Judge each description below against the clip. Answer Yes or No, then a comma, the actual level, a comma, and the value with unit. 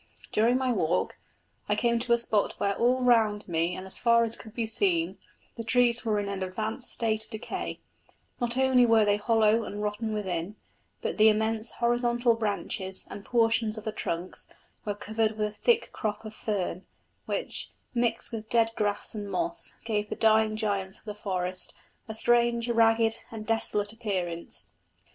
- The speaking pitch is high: Yes, high, 220 Hz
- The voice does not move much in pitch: Yes, narrow, 2.2 semitones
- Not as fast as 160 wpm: No, average, 175 wpm